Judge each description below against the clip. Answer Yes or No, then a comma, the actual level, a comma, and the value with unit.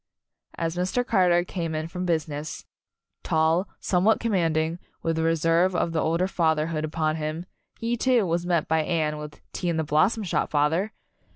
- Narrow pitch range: Yes, narrow, 2.3 semitones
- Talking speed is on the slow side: No, average, 175 wpm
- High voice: No, medium, 165 Hz